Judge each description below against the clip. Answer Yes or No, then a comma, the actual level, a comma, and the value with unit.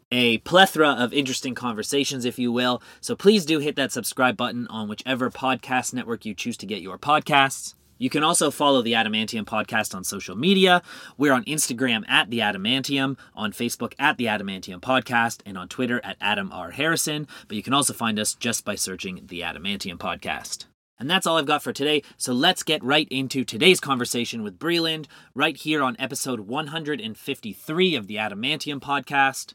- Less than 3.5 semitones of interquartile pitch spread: No, average, 4.6 semitones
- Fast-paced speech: No, average, 185 wpm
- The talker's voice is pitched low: Yes, low, 130 Hz